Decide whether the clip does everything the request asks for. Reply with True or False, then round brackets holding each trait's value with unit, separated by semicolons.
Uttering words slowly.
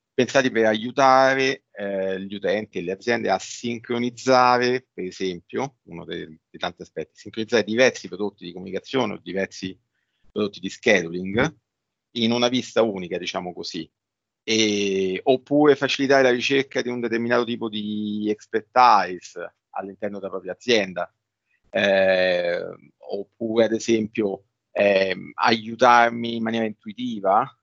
False (125 wpm)